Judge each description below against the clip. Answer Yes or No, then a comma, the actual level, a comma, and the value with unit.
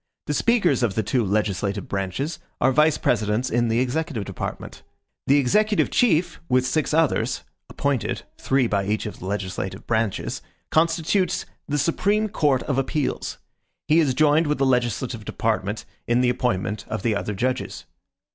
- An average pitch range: No, wide, 6.1 semitones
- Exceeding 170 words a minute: No, average, 155 wpm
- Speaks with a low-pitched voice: Yes, low, 125 Hz